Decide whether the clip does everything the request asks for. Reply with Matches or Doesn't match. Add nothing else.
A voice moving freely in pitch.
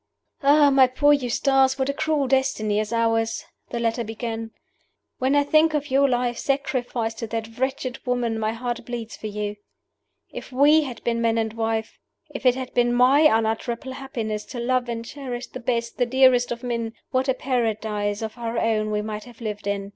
Doesn't match